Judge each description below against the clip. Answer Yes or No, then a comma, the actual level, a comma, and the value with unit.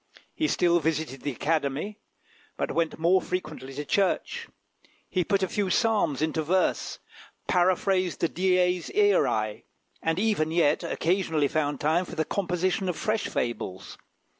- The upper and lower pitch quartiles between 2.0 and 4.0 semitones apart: Yes, average, 3.5 semitones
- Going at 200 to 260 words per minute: No, average, 145 wpm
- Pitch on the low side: No, medium, 175 Hz